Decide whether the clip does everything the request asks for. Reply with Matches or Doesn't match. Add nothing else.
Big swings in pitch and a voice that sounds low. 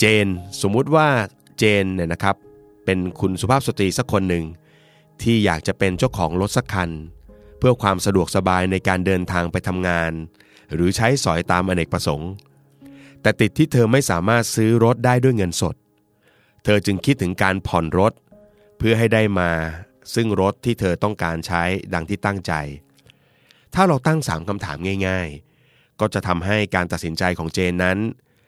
Doesn't match